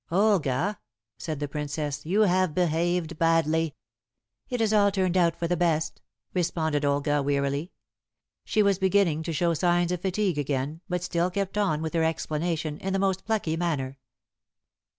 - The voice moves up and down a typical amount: Yes, average, 3.6 semitones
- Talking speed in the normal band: Yes, average, 160 wpm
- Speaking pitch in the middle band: Yes, medium, 170 Hz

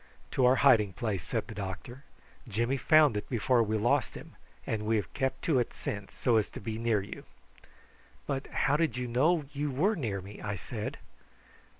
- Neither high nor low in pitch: No, low, 120 Hz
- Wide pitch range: No, average, 4.3 semitones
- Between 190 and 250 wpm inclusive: Yes, average, 195 wpm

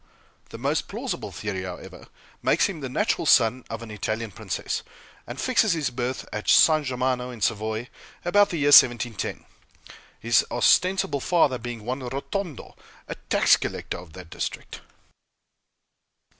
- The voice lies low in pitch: Yes, low, 125 Hz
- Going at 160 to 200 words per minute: No, average, 145 wpm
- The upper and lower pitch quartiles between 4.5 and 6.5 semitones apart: Yes, average, 5.2 semitones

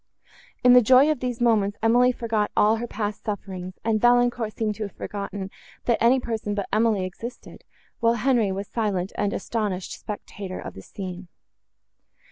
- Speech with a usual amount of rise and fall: Yes, average, 3.0 semitones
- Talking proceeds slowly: No, average, 170 wpm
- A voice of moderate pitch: No, high, 215 Hz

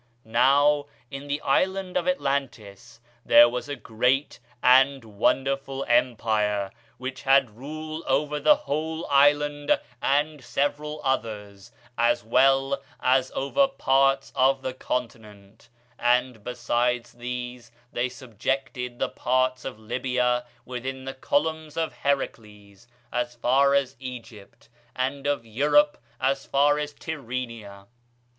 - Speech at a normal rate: No, slow, 120 wpm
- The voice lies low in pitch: Yes, low, 130 Hz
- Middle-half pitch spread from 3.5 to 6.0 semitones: No, average, 2.9 semitones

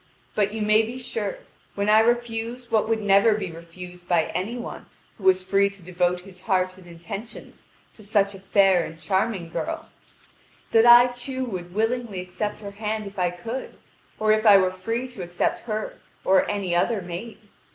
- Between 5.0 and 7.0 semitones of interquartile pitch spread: No, average, 3.5 semitones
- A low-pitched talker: No, high, 200 Hz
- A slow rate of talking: No, average, 185 wpm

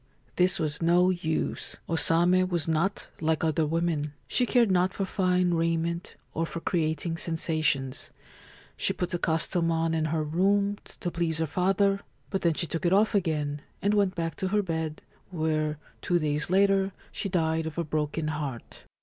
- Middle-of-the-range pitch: Yes, medium, 165 Hz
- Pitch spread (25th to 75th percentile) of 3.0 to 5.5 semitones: No, narrow, 2.6 semitones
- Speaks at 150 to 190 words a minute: Yes, average, 175 wpm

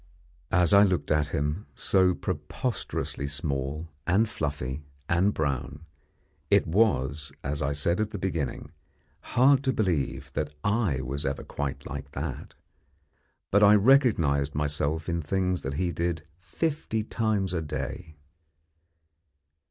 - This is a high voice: No, very low, 80 Hz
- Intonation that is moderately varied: No, wide, 5.7 semitones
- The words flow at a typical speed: No, slow, 130 wpm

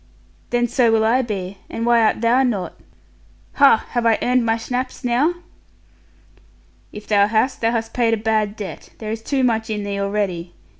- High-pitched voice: Yes, high, 225 Hz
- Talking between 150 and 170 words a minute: No, average, 185 wpm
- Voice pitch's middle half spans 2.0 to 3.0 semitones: Yes, narrow, 2.4 semitones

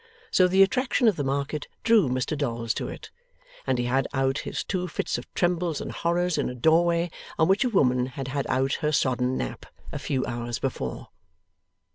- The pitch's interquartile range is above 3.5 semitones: Yes, wide, 5.4 semitones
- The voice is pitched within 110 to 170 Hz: Yes, medium, 140 Hz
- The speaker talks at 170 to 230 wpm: Yes, average, 195 wpm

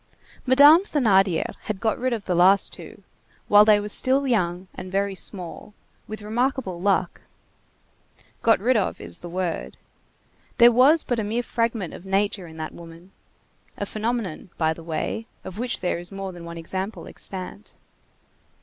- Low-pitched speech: No, high, 200 Hz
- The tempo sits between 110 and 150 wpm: No, average, 165 wpm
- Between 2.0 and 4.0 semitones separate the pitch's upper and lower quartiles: No, average, 4.4 semitones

